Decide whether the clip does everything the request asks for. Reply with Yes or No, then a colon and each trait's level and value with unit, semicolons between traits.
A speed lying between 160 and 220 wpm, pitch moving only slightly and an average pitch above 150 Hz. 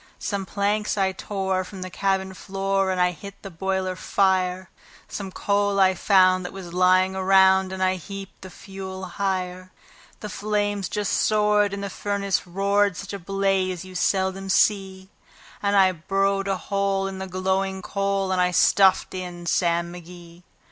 Yes: average, 165 wpm; narrow, 1.2 semitones; high, 190 Hz